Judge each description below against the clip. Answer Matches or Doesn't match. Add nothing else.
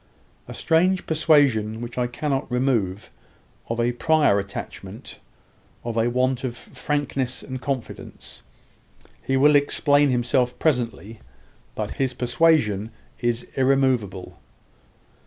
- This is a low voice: Matches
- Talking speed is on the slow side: Matches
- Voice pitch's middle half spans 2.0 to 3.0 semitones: Doesn't match